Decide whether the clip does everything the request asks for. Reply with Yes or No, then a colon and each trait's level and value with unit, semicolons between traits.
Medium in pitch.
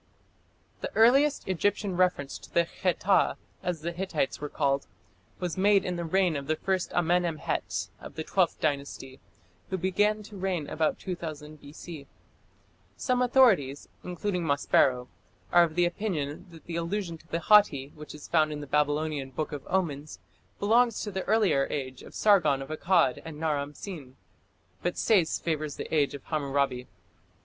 Yes: medium, 165 Hz